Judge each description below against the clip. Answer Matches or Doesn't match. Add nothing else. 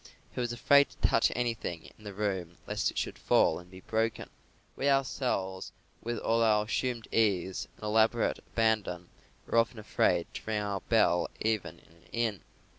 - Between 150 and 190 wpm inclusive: Matches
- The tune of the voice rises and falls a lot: Doesn't match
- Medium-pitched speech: Doesn't match